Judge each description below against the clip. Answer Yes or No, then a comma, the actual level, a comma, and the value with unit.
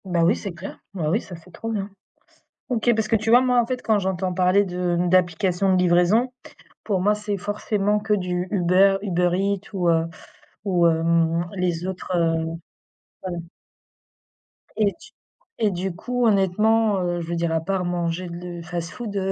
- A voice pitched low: No, medium, 185 Hz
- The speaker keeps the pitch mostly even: No, average, 3.0 semitones